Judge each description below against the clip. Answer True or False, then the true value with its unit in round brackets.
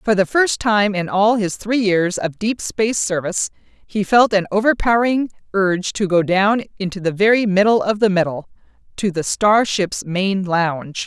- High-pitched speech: True (200 Hz)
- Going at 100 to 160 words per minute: False (180 wpm)